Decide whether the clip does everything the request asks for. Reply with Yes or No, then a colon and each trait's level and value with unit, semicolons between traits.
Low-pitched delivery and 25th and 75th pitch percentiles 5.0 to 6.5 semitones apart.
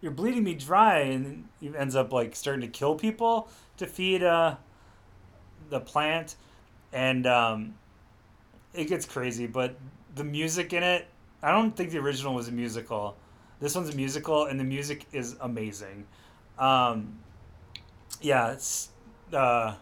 Yes: low, 125 Hz; wide, 5.5 semitones